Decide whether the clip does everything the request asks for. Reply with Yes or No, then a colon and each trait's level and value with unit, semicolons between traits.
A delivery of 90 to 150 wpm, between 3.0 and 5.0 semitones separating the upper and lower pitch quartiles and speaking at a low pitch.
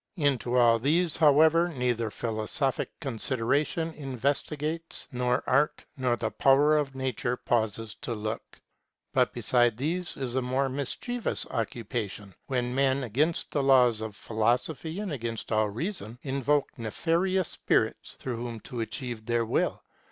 Yes: slow, 135 wpm; average, 4.1 semitones; low, 130 Hz